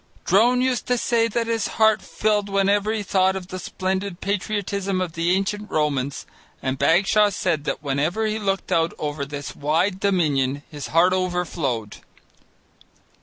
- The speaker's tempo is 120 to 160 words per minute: Yes, average, 155 wpm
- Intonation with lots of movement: No, average, 4.9 semitones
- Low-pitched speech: No, medium, 185 Hz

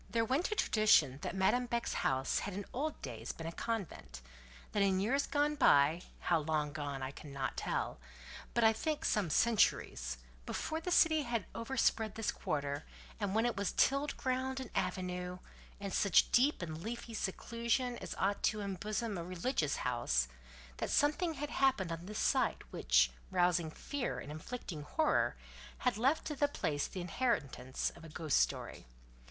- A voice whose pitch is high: Yes, high, 200 Hz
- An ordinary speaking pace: Yes, average, 170 wpm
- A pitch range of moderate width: No, wide, 8.5 semitones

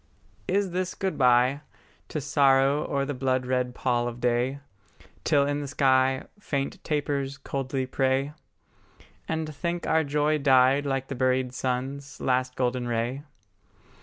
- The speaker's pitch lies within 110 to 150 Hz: Yes, low, 135 Hz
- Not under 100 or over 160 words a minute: Yes, average, 140 wpm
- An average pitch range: No, narrow, 2.1 semitones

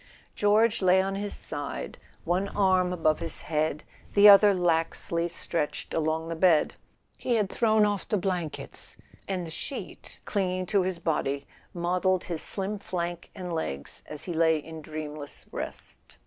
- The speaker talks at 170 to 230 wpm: No, average, 155 wpm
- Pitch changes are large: No, average, 3.3 semitones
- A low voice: No, medium, 175 Hz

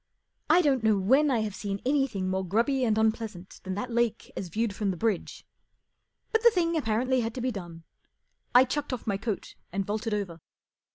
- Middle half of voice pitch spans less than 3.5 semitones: No, average, 4.6 semitones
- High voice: Yes, high, 220 Hz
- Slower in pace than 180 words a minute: No, average, 195 wpm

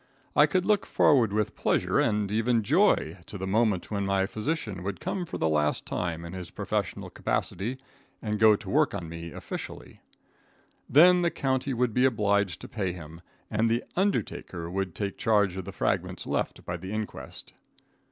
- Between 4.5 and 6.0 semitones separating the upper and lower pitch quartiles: Yes, average, 5.0 semitones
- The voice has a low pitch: Yes, low, 105 Hz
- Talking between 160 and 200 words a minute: Yes, average, 180 wpm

